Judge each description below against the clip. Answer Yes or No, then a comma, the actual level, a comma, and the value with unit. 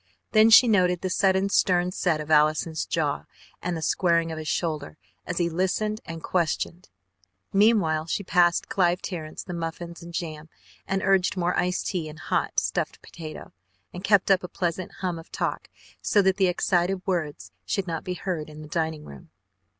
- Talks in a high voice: No, medium, 175 Hz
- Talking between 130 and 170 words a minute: No, average, 180 wpm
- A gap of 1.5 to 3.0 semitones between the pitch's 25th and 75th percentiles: Yes, average, 2.7 semitones